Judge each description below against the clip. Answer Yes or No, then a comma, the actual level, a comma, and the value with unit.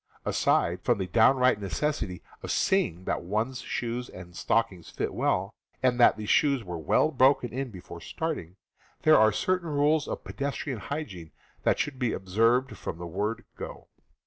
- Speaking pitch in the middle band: No, low, 115 Hz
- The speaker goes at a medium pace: Yes, average, 165 wpm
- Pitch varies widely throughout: Yes, wide, 6.8 semitones